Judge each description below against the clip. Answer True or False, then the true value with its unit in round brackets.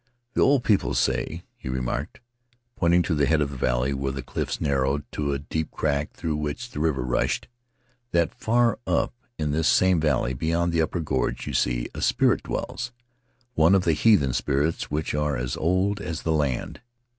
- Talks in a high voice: False (75 Hz)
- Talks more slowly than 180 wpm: False (190 wpm)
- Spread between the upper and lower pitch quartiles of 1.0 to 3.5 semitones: False (4.0 semitones)